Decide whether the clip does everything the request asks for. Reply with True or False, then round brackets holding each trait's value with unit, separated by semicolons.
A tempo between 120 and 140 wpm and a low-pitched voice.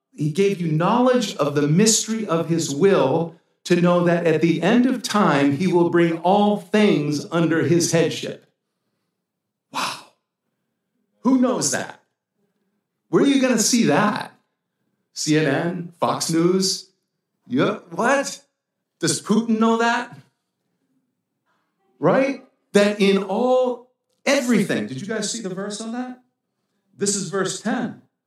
False (135 wpm; 200 Hz)